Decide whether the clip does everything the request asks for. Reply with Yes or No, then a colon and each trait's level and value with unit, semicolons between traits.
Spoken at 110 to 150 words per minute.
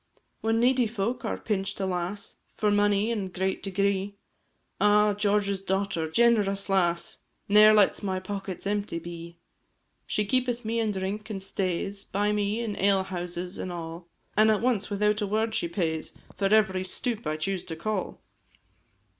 No: average, 165 wpm